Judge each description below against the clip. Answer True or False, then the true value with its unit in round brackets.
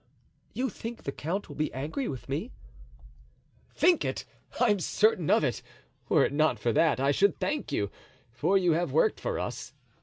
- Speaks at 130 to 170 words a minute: False (180 wpm)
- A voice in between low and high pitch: True (175 Hz)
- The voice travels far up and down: True (8.2 semitones)